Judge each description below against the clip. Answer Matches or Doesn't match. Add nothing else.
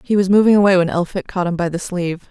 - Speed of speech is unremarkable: Doesn't match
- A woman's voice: Matches